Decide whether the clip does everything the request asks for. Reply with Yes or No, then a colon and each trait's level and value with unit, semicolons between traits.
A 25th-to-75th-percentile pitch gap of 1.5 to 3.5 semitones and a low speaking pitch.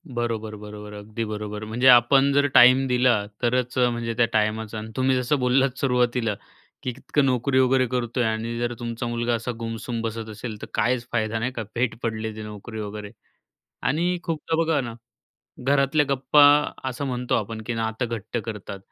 Yes: narrow, 2.5 semitones; low, 120 Hz